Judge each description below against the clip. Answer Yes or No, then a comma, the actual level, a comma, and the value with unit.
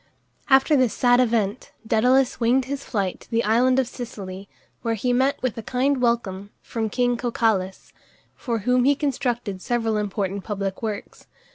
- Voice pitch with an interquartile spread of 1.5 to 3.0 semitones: No, average, 3.5 semitones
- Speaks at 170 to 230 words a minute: No, average, 160 wpm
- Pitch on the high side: Yes, high, 235 Hz